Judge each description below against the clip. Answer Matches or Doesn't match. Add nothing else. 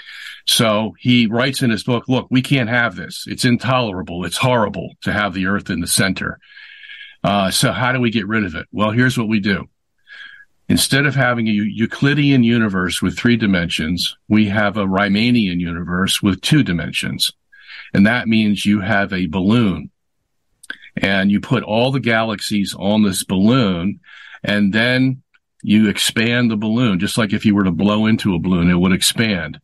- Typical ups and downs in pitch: Matches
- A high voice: Doesn't match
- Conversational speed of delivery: Matches